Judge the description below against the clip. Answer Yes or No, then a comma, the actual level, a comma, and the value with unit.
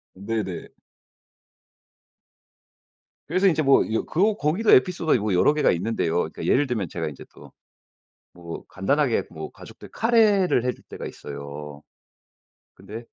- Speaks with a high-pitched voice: No, low, 115 Hz